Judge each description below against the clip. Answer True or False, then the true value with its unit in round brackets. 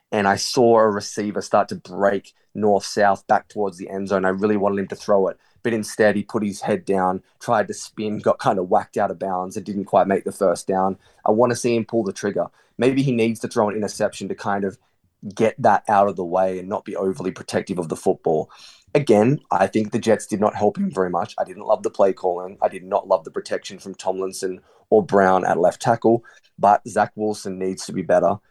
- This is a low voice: True (100 Hz)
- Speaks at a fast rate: True (240 wpm)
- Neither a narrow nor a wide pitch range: False (2.2 semitones)